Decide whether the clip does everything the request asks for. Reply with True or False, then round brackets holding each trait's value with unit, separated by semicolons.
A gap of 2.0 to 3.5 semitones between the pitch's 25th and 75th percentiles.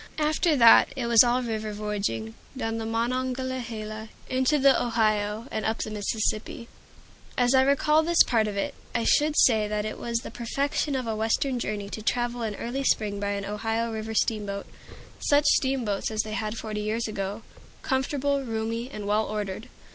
True (3.2 semitones)